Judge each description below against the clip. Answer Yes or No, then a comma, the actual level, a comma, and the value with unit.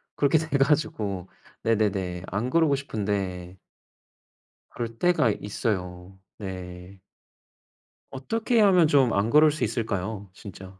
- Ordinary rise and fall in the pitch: No, wide, 7.0 semitones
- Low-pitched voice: Yes, low, 110 Hz